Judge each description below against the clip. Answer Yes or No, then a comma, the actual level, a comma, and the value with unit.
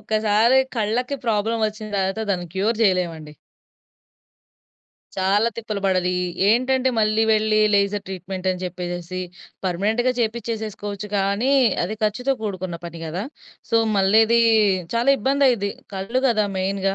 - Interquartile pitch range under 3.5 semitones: Yes, average, 3.0 semitones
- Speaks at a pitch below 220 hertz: Yes, high, 210 Hz